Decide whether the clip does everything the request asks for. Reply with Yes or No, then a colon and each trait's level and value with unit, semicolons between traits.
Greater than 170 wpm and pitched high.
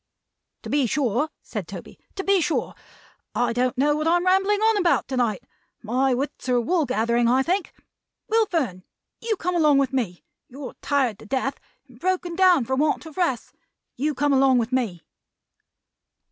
Yes: average, 180 wpm; very high, 275 Hz